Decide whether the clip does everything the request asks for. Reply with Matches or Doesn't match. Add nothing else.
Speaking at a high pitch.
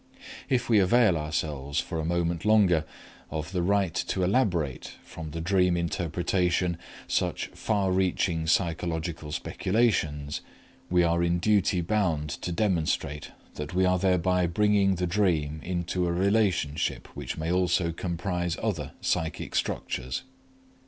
Doesn't match